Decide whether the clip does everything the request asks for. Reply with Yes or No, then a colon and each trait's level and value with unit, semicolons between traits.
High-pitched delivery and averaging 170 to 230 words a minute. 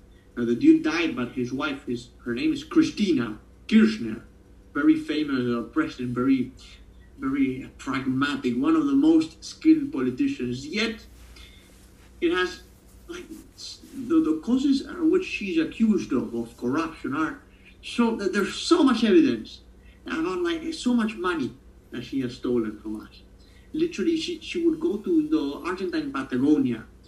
No: high, 220 Hz; average, 150 wpm